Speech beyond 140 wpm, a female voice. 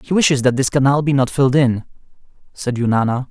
No: average, 200 wpm; male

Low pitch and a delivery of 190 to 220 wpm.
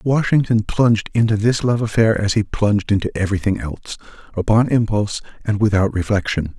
No: low, 105 Hz; average, 145 wpm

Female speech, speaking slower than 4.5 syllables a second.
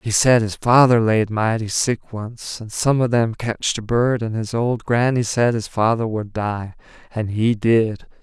No: male; 4.2 syllables/s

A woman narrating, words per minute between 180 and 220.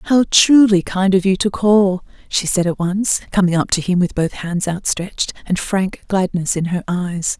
Yes: female; fast, 205 wpm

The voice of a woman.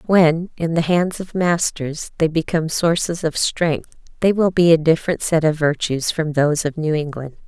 Yes: female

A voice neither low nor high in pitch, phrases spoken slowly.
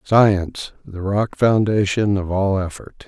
No: low, 100 Hz; slow, 115 wpm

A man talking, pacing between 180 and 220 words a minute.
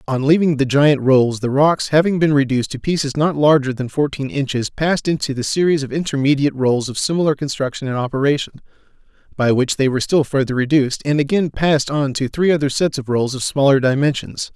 Yes: male; average, 200 wpm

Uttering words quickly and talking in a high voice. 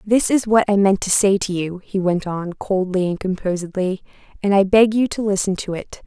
Yes: fast, 230 wpm; high, 195 Hz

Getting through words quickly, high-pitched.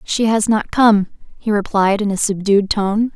No: average, 190 wpm; high, 210 Hz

